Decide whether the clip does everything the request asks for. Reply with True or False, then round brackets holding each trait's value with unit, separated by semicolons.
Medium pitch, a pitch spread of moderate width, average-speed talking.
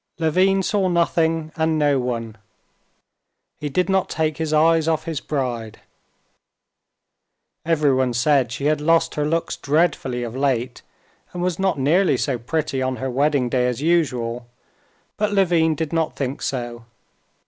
True (150 Hz; 4.2 semitones; 150 wpm)